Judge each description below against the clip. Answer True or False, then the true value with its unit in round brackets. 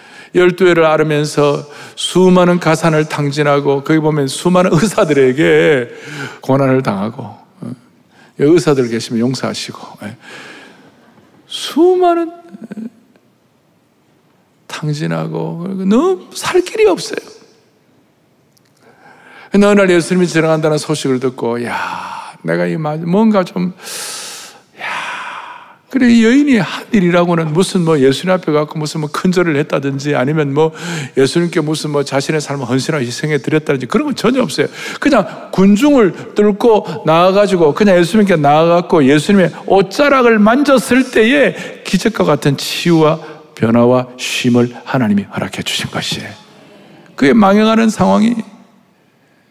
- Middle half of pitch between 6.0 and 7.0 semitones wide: True (6.7 semitones)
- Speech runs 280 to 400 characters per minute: False (270 characters per minute)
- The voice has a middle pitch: True (175 Hz)